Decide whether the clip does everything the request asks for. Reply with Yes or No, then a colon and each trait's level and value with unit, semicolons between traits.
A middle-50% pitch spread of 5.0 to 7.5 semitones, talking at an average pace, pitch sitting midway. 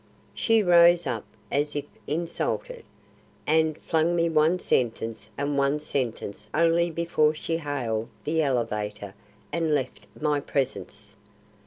No: average, 5.3 semitones; slow, 125 wpm; medium, 150 Hz